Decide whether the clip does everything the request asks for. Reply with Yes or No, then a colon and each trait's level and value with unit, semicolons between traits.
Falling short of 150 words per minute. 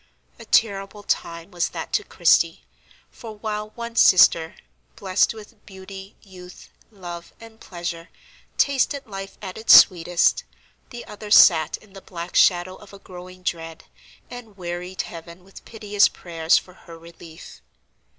Yes: average, 140 wpm